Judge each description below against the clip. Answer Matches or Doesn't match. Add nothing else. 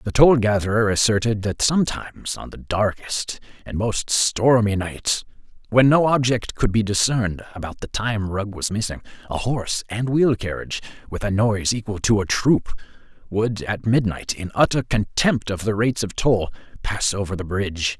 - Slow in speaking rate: Doesn't match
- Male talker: Matches